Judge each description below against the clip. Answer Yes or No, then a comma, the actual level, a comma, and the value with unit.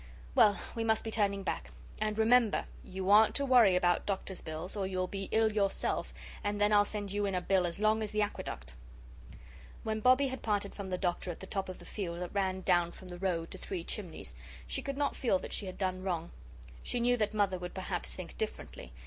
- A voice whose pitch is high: Yes, high, 195 Hz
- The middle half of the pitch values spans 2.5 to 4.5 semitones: Yes, average, 2.8 semitones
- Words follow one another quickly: Yes, fast, 225 wpm